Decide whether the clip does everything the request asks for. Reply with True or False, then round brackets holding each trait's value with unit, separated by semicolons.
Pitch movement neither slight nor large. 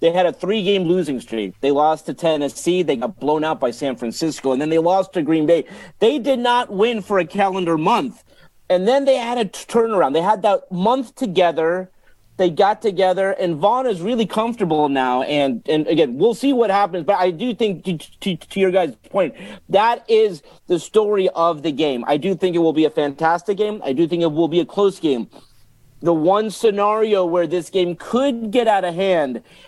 True (4.8 semitones)